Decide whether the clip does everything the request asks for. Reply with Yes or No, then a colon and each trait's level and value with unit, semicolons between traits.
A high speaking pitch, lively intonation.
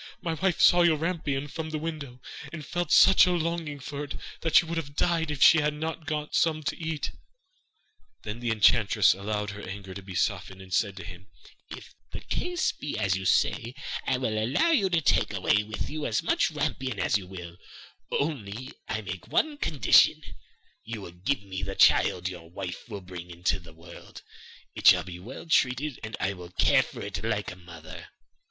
No: low, 115 Hz; wide, 8.4 semitones